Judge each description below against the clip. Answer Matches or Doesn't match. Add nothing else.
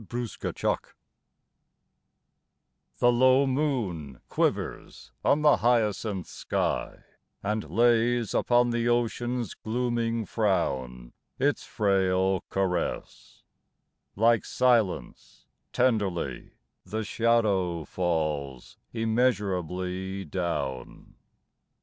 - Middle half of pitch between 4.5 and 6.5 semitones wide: Matches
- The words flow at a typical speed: Doesn't match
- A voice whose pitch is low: Matches